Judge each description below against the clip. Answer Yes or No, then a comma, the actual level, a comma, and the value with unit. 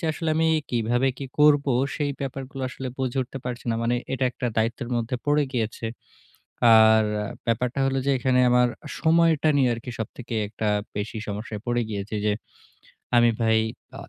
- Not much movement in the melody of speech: No, average, 3.1 semitones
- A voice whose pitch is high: No, low, 125 Hz